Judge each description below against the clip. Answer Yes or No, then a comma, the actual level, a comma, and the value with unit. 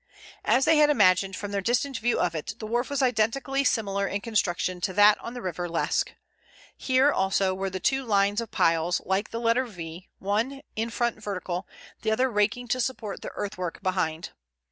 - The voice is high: Yes, high, 210 Hz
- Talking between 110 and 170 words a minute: No, average, 190 wpm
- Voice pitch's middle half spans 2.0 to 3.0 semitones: No, average, 4.4 semitones